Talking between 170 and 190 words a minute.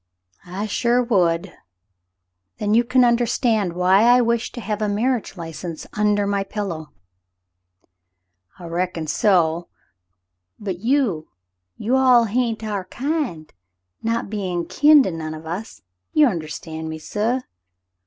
No: average, 155 wpm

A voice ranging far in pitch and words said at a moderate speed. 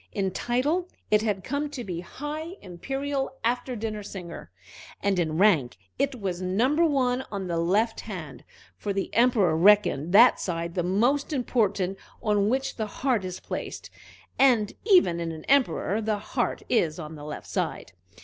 Yes: wide, 6.1 semitones; average, 165 wpm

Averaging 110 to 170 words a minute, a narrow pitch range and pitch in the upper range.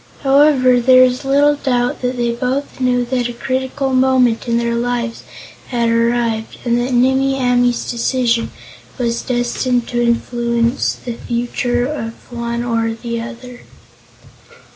Yes: average, 140 wpm; narrow, 1.5 semitones; high, 245 Hz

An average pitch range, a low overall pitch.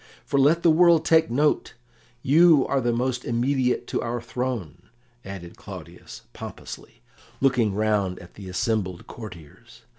No: wide, 5.9 semitones; low, 120 Hz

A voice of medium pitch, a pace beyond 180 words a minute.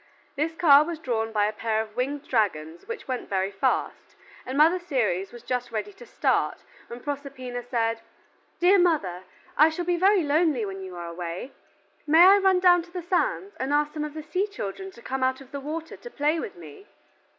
No: very high, 280 Hz; fast, 205 wpm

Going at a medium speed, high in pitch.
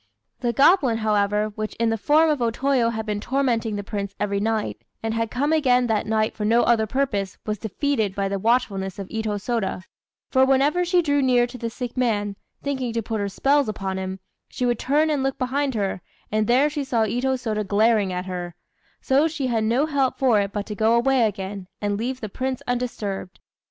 No: fast, 215 wpm; high, 230 Hz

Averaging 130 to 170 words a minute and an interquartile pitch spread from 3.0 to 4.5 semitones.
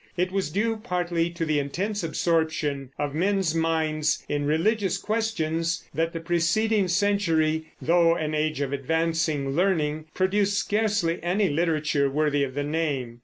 Yes: average, 145 wpm; average, 3.6 semitones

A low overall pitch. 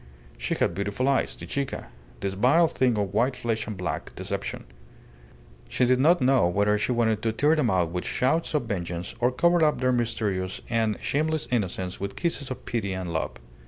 Yes: low, 115 Hz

